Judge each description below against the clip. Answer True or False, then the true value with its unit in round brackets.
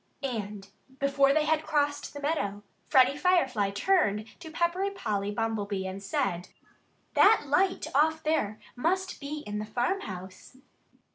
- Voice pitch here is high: True (275 Hz)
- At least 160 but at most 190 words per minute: False (135 wpm)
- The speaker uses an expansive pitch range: True (7.5 semitones)